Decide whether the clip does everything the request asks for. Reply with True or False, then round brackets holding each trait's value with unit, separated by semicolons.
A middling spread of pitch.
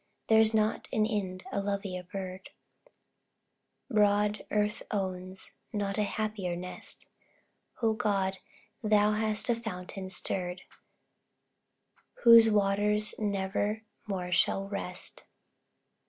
False (2.1 semitones)